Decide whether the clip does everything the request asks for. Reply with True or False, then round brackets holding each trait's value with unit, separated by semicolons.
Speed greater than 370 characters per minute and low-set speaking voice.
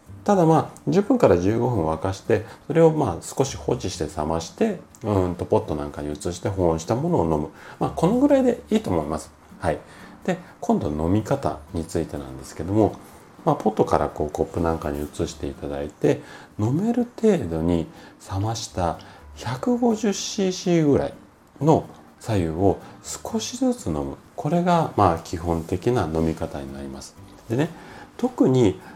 False (315 characters per minute; 90 Hz)